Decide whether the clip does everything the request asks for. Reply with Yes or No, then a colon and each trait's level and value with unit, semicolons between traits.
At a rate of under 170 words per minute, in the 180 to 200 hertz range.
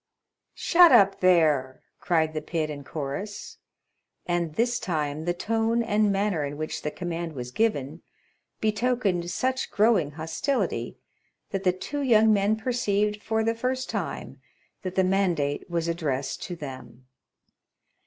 Yes: average, 140 wpm; medium, 185 Hz